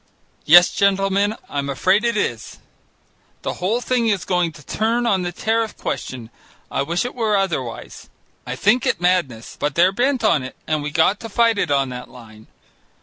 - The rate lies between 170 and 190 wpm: Yes, average, 185 wpm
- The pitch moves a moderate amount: No, wide, 7.3 semitones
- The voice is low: No, medium, 185 Hz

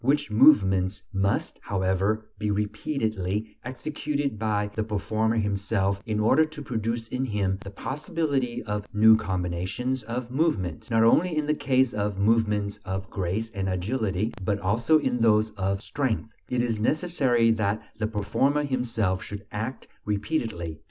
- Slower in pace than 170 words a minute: Yes, average, 145 wpm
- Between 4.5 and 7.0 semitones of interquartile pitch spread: No, average, 4.0 semitones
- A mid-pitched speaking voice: No, low, 110 Hz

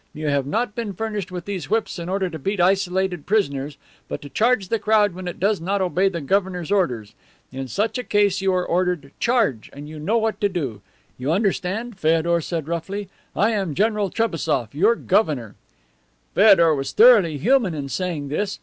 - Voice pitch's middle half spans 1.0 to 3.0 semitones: No, average, 4.7 semitones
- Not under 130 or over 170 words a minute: No, average, 190 wpm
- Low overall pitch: No, medium, 185 Hz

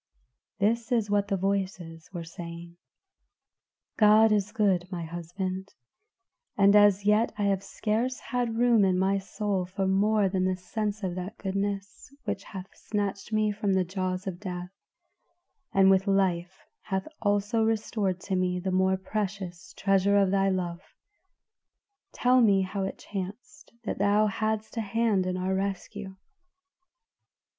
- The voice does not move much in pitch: Yes, narrow, 2.0 semitones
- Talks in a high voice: Yes, high, 195 Hz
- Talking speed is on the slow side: No, average, 150 wpm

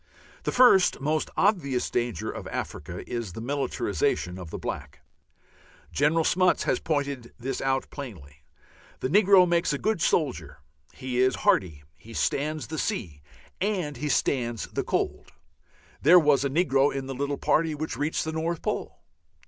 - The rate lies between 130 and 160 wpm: Yes, average, 155 wpm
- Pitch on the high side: No, medium, 140 Hz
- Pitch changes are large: No, average, 4.9 semitones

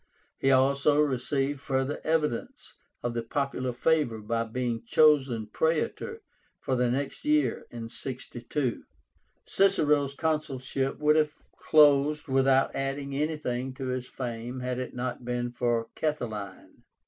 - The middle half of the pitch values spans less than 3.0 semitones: No, average, 3.5 semitones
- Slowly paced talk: Yes, slow, 125 wpm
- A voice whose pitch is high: No, low, 135 Hz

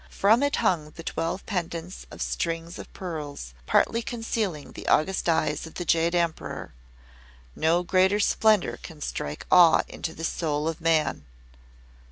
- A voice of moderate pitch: Yes, medium, 170 Hz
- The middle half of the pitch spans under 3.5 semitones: Yes, average, 2.8 semitones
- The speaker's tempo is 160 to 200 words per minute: No, average, 150 wpm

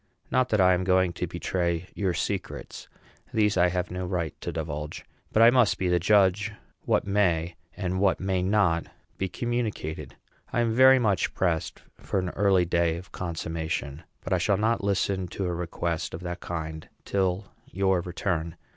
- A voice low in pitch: Yes, very low, 90 Hz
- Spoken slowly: No, average, 175 wpm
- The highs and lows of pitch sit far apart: No, narrow, 2.6 semitones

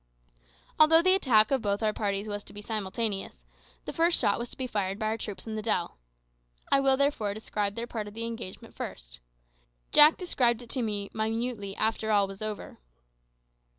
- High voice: Yes, high, 220 Hz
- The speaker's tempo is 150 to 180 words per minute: No, average, 190 wpm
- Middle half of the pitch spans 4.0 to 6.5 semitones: No, average, 2.9 semitones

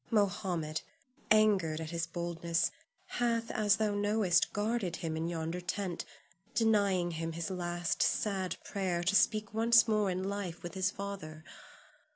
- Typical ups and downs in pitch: Yes, average, 3.5 semitones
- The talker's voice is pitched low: No, medium, 185 Hz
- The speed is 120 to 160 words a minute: Yes, average, 145 wpm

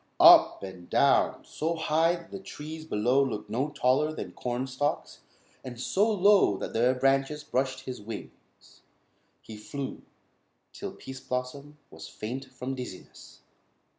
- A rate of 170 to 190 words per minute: No, average, 140 wpm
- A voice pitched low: Yes, low, 130 Hz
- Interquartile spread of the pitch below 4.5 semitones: Yes, average, 3.4 semitones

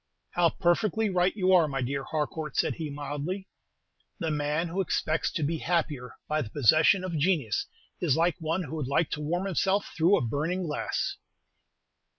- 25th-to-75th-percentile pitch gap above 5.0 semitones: No, average, 3.5 semitones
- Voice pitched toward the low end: No, medium, 160 Hz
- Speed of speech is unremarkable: Yes, average, 175 wpm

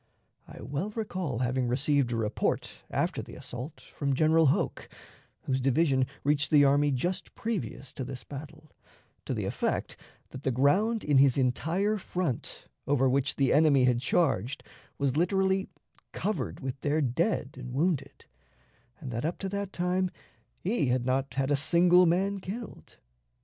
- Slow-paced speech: No, average, 155 wpm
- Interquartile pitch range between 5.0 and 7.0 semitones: Yes, average, 5.3 semitones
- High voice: No, medium, 145 Hz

